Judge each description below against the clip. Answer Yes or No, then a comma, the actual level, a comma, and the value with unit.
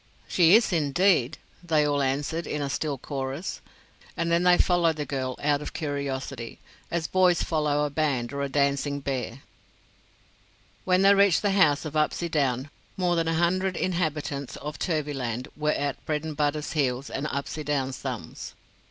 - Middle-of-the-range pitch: Yes, medium, 150 Hz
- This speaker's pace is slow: No, average, 155 wpm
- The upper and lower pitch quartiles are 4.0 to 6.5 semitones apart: No, average, 3.2 semitones